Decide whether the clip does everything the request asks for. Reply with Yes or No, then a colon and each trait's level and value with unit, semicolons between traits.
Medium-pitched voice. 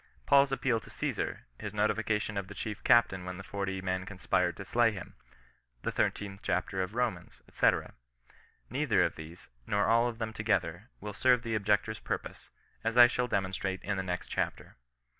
No: low, 100 Hz